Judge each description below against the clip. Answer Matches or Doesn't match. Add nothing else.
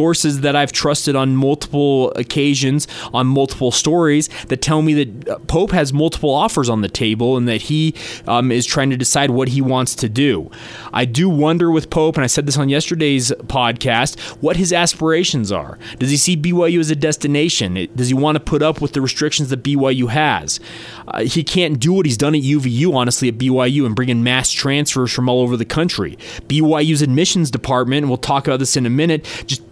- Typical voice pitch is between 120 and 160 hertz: Matches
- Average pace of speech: Doesn't match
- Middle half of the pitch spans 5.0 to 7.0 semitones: Doesn't match